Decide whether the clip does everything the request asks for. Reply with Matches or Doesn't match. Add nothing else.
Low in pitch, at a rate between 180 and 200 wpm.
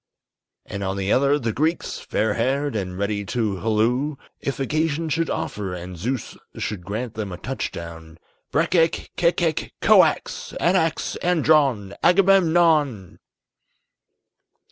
Doesn't match